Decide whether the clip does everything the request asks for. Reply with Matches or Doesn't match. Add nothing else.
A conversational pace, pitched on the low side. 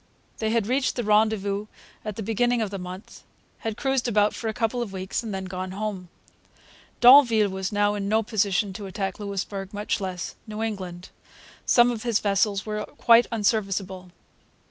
Doesn't match